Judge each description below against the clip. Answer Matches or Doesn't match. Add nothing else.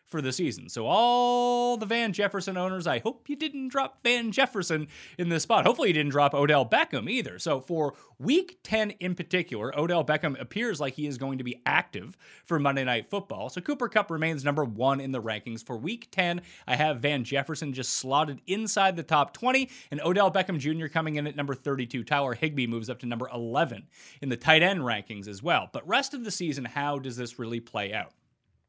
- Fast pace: Matches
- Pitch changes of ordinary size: Doesn't match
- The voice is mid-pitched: Matches